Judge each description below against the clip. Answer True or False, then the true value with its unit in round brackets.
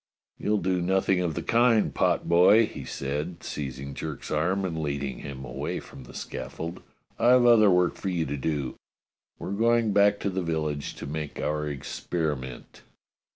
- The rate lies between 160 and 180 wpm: True (165 wpm)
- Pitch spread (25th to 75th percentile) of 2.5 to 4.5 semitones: False (5.4 semitones)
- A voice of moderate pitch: False (85 Hz)